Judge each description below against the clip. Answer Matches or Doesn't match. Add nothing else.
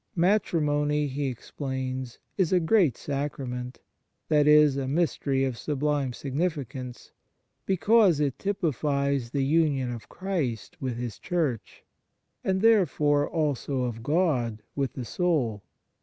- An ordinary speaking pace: Doesn't match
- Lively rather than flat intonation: Doesn't match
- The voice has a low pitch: Doesn't match